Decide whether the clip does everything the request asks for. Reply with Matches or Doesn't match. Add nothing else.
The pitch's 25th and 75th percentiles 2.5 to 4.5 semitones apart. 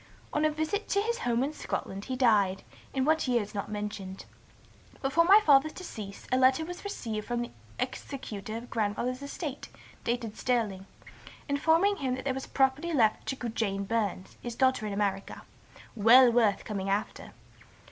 Doesn't match